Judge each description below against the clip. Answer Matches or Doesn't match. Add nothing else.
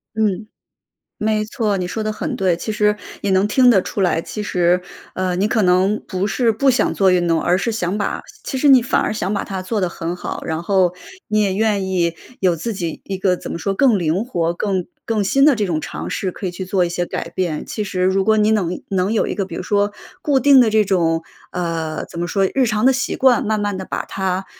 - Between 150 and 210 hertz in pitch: Matches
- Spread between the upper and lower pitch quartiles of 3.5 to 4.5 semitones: Doesn't match